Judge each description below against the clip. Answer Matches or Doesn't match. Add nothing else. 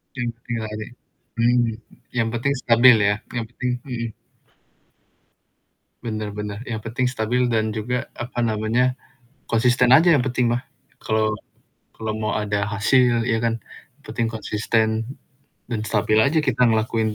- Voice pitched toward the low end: Matches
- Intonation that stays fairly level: Matches